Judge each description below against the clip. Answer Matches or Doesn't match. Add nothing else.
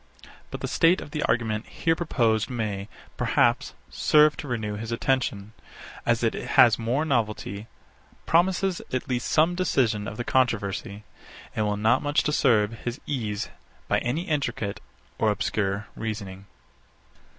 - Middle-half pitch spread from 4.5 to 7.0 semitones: Matches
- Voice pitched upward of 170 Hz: Doesn't match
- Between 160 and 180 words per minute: Doesn't match